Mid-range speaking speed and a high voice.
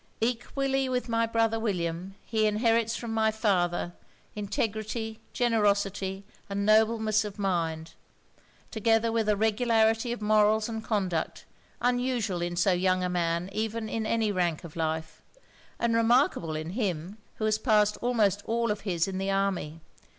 Yes: average, 145 wpm; high, 215 Hz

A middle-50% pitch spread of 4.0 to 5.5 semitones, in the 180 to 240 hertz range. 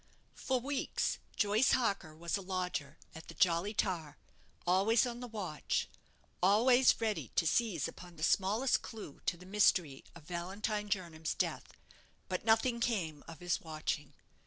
Yes: average, 4.9 semitones; high, 190 Hz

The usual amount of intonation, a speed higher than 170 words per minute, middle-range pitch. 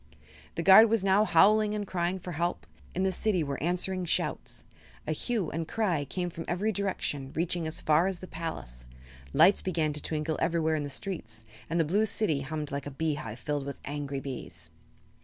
Yes: average, 4.4 semitones; average, 195 wpm; medium, 165 Hz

